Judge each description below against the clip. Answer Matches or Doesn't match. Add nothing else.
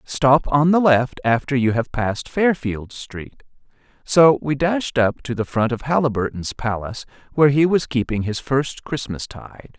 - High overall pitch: Doesn't match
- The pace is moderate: Matches